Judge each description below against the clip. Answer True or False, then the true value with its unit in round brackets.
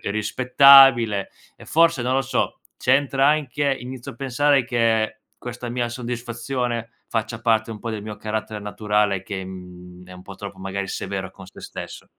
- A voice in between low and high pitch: False (115 Hz)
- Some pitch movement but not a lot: True (3.9 semitones)